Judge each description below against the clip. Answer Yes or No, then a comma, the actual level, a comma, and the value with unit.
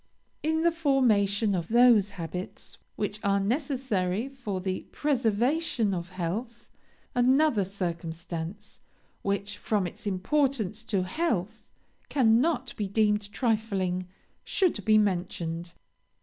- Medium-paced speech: No, slow, 105 wpm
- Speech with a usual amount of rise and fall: Yes, average, 5.0 semitones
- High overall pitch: Yes, high, 210 Hz